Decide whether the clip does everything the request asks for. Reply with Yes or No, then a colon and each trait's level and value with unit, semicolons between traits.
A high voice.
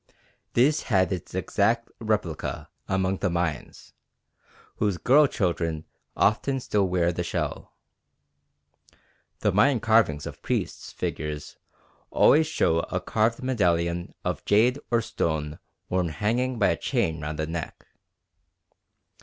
No: very low, 95 Hz